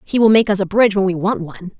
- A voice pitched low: No, high, 200 Hz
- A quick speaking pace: Yes, fast, 335 wpm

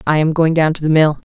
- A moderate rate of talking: No, fast, 320 wpm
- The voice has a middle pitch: Yes, medium, 155 Hz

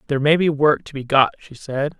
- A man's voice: Yes, male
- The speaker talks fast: Yes, fast, 270 wpm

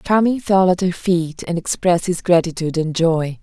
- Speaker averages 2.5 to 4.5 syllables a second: No, 5.0 syllables/s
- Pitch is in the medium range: Yes, medium, 175 Hz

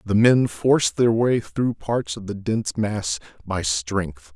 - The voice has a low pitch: Yes, low, 105 Hz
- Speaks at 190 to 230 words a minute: No, average, 180 wpm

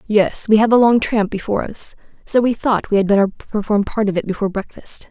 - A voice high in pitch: Yes, high, 210 Hz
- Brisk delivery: Yes, fast, 235 wpm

